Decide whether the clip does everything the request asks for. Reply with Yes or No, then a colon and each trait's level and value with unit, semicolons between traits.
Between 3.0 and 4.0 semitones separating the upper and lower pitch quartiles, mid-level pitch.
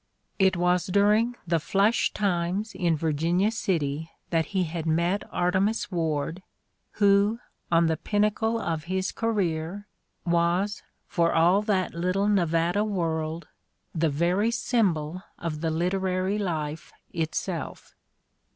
Yes: average, 3.6 semitones; medium, 180 Hz